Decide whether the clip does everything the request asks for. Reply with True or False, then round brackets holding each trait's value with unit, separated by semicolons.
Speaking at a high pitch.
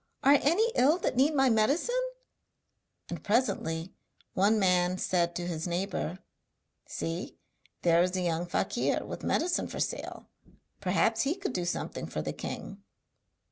True (195 Hz)